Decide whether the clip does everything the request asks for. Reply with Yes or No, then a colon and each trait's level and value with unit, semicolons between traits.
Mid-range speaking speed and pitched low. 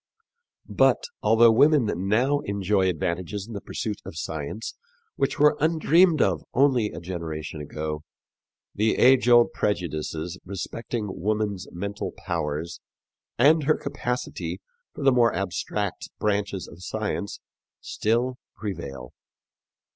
No: slow, 115 wpm; low, 105 Hz